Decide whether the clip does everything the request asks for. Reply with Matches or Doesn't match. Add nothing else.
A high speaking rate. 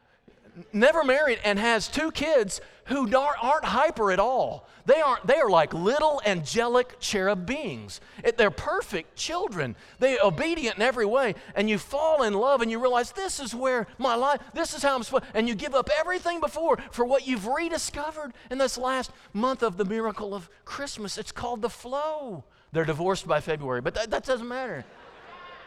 Doesn't match